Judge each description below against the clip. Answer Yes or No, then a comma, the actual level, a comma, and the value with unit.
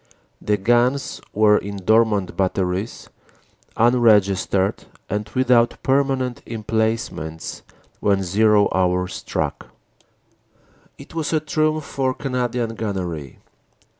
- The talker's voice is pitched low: Yes, low, 110 Hz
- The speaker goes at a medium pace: No, slow, 100 wpm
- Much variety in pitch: No, average, 4.5 semitones